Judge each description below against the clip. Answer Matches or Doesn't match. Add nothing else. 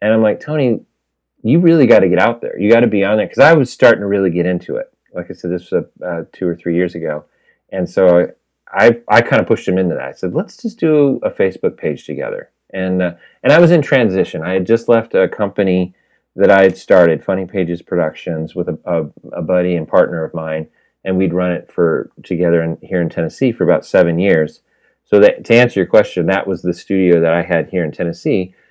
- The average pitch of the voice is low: Matches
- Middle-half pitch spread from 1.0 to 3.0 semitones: Doesn't match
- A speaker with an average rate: Doesn't match